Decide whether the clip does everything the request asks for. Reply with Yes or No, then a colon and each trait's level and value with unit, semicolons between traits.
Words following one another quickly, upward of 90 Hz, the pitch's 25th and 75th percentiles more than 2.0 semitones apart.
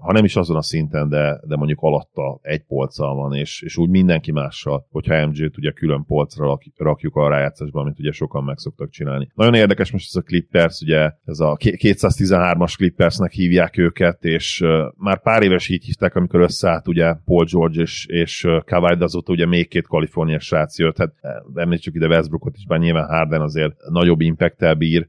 No: fast, 190 wpm; very low, 85 Hz; narrow, 2.4 semitones